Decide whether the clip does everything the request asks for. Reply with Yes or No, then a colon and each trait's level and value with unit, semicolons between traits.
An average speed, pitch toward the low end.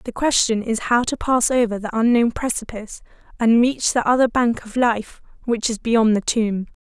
No: average, 195 wpm; high, 230 Hz